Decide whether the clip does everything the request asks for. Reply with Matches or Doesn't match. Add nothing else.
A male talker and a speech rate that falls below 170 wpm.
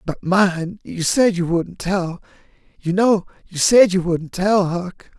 Doesn't match